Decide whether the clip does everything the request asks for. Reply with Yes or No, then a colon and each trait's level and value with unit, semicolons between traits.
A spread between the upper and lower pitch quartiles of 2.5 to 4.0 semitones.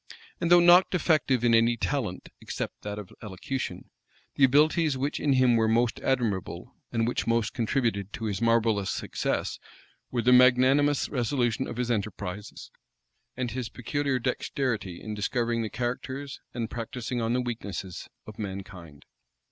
Yes: average, 3.4 semitones